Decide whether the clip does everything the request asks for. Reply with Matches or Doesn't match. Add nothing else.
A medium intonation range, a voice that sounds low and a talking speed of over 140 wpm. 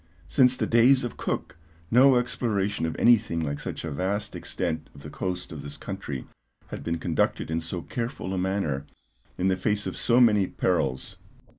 Doesn't match